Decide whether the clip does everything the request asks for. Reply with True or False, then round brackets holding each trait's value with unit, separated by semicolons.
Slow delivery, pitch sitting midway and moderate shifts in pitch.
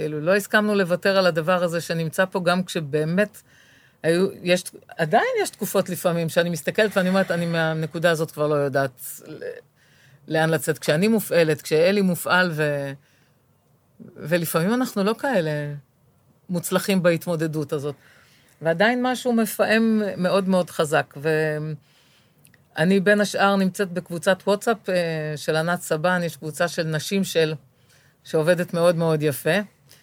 False (130 wpm; 175 Hz; 3.9 semitones)